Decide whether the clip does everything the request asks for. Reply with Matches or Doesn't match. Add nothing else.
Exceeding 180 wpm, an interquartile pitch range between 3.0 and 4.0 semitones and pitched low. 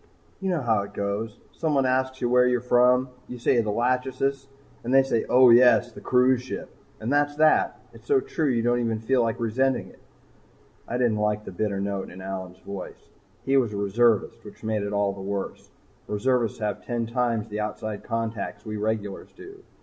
Matches